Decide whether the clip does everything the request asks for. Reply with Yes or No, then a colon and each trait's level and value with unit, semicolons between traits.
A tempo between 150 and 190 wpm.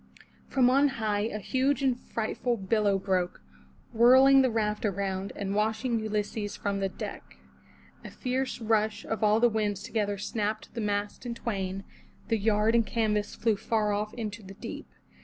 Yes: average, 165 wpm